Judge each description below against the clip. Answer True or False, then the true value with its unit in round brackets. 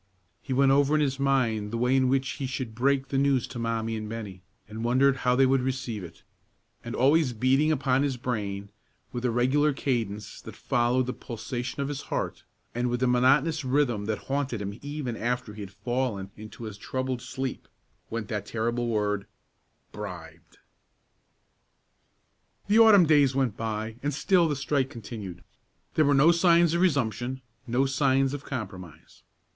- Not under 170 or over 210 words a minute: True (175 wpm)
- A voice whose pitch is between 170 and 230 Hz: False (125 Hz)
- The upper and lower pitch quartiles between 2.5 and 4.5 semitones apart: True (3.7 semitones)